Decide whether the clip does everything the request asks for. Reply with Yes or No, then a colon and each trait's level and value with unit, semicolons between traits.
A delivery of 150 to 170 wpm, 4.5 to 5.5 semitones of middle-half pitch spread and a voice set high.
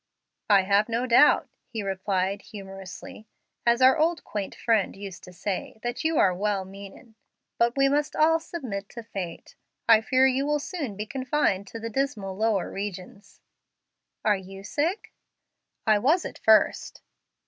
Yes: average, 160 wpm; average, 4.9 semitones; high, 215 Hz